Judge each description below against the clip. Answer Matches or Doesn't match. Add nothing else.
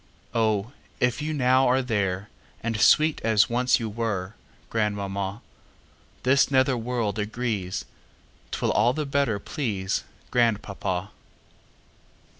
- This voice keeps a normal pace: Doesn't match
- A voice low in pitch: Matches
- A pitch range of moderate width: Matches